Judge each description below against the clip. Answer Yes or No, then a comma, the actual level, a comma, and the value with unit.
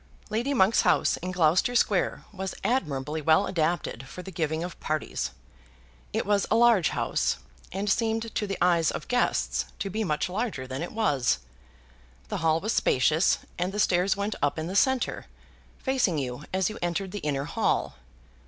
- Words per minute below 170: No, average, 175 wpm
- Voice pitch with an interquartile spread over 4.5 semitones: Yes, average, 5.0 semitones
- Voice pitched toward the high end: No, medium, 180 Hz